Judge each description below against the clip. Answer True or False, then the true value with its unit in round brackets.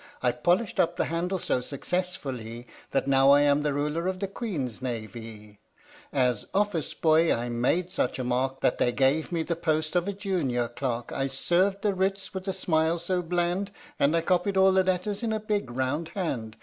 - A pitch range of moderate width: False (6.3 semitones)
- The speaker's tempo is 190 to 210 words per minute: True (200 wpm)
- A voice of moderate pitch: True (160 Hz)